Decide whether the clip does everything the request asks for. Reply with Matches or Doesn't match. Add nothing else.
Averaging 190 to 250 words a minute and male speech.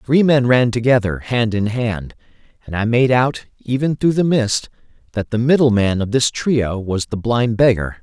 Matches